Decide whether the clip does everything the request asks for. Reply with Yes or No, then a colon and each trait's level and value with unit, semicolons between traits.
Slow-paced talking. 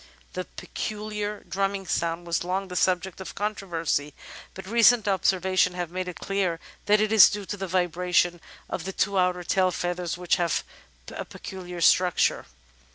No: average, 160 wpm